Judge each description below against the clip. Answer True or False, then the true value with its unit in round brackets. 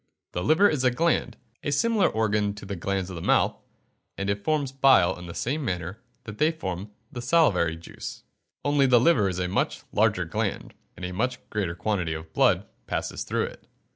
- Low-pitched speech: True (105 Hz)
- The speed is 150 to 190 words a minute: False (200 wpm)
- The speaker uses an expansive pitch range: True (7.0 semitones)